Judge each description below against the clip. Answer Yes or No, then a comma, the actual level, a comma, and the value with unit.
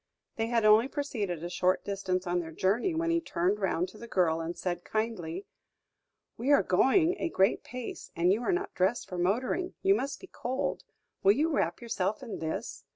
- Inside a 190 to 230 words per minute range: Yes, average, 200 wpm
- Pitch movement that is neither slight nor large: No, wide, 6.6 semitones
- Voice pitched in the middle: No, high, 210 Hz